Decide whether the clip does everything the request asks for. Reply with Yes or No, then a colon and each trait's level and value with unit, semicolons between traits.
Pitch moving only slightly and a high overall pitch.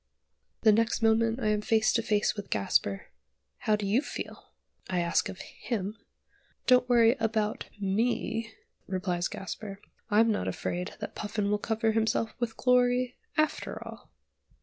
Yes: narrow, 2.0 semitones; high, 220 Hz